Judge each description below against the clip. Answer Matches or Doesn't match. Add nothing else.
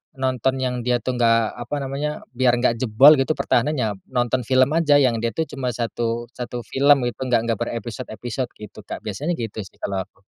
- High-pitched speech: Doesn't match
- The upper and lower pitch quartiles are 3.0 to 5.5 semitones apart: Doesn't match